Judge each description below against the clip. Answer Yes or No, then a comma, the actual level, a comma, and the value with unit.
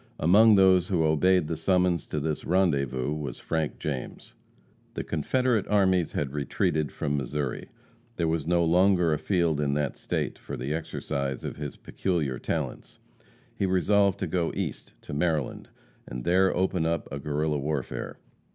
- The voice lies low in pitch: Yes, very low, 80 Hz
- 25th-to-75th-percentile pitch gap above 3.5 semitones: Yes, average, 4.1 semitones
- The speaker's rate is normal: Yes, average, 160 wpm